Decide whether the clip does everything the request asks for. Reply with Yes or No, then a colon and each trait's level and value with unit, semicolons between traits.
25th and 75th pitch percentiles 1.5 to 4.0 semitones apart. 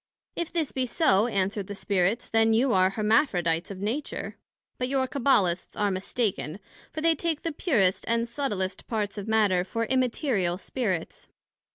No: wide, 5.4 semitones